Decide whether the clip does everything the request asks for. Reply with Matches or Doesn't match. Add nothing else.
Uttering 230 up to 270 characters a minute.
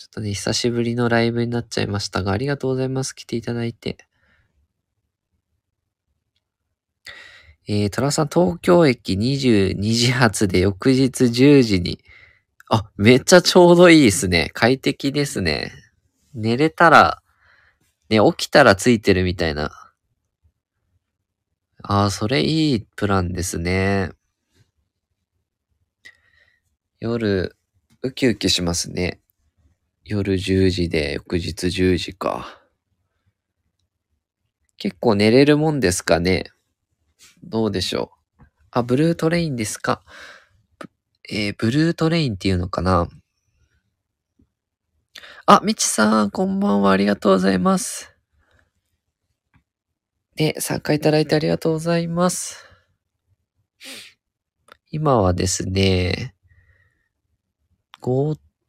Doesn't match